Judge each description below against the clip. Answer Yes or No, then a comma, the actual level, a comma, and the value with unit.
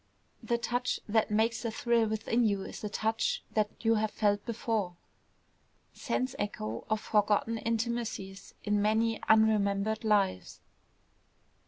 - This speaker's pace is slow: Yes, slow, 130 wpm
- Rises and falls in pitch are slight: Yes, narrow, 1.7 semitones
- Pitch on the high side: Yes, high, 220 Hz